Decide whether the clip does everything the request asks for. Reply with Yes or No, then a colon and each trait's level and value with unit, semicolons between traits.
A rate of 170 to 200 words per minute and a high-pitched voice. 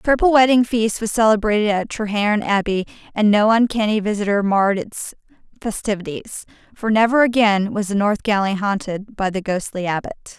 No: average, 160 wpm; high, 210 Hz